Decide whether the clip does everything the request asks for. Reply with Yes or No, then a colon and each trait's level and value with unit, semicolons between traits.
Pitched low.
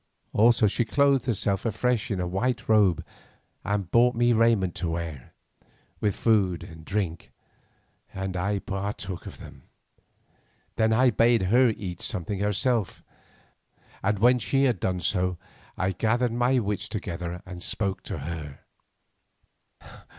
Yes: low, 100 Hz